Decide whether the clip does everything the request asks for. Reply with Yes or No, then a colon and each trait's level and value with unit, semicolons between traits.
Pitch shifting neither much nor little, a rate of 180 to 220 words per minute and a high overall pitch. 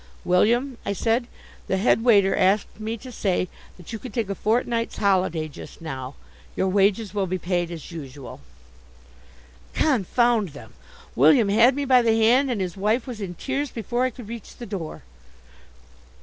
No: average, 4.6 semitones; average, 170 wpm; high, 210 Hz